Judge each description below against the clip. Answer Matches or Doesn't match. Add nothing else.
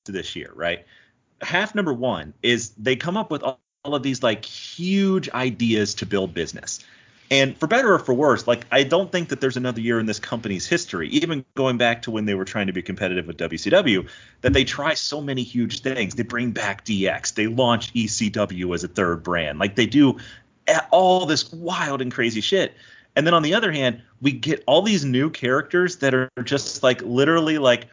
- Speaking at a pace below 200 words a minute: Doesn't match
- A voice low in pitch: Matches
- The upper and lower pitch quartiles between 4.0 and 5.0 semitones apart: Matches